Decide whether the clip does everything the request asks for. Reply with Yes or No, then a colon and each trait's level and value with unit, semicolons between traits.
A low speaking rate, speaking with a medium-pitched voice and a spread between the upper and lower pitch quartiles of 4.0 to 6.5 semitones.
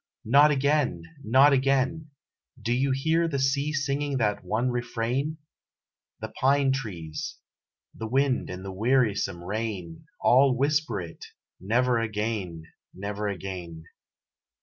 No: slow, 120 wpm; low, 120 Hz; wide, 5.4 semitones